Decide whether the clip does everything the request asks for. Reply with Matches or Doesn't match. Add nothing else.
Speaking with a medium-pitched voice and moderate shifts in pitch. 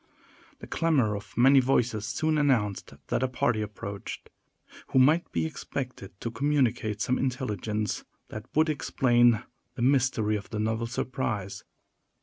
Doesn't match